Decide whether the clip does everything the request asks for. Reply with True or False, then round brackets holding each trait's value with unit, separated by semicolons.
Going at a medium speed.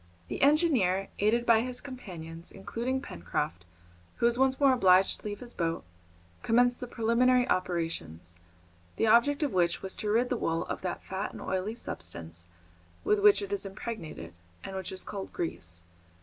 True (170 wpm)